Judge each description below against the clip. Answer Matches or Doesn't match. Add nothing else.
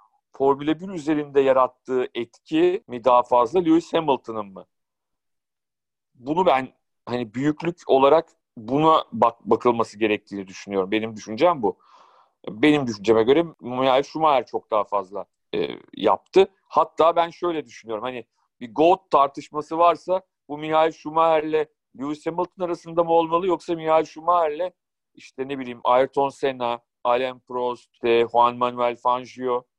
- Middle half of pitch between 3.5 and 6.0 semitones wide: Matches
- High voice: Doesn't match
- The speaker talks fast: Doesn't match